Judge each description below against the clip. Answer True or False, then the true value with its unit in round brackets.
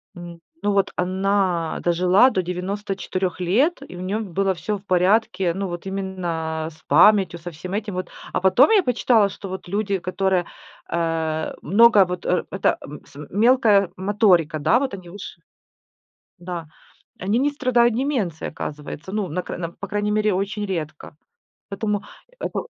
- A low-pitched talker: False (190 Hz)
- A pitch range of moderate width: True (3.1 semitones)